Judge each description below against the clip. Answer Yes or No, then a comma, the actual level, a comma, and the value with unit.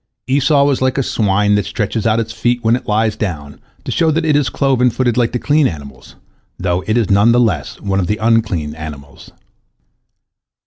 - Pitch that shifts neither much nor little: Yes, average, 4.6 semitones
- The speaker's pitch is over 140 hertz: No, low, 110 Hz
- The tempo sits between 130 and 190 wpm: No, fast, 205 wpm